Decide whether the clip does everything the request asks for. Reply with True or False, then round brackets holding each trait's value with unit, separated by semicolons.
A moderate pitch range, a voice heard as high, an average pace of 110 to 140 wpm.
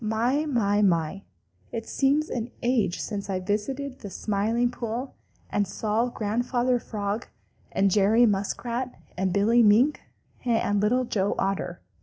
True (3.4 semitones; 220 Hz; 135 wpm)